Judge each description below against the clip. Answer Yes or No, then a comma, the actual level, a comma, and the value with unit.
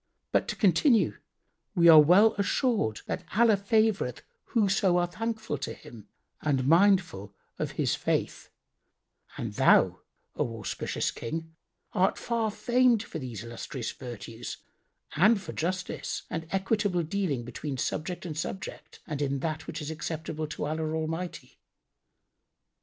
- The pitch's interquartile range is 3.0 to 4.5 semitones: No, average, 5.3 semitones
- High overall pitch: No, medium, 165 Hz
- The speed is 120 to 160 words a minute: Yes, slow, 135 wpm